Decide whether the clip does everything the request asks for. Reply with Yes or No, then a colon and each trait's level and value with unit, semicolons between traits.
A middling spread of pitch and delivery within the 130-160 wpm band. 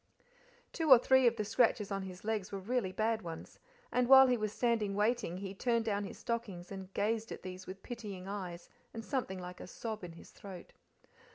No: average, 3.7 semitones; fast, 205 wpm